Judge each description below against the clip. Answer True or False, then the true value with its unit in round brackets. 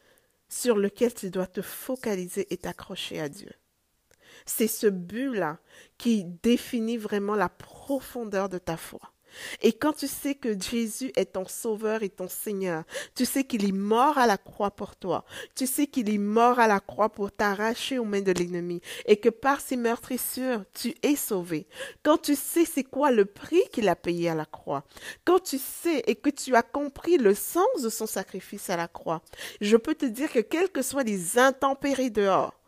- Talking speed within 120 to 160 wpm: False (195 wpm)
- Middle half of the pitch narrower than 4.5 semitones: False (5.5 semitones)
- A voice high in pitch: True (230 Hz)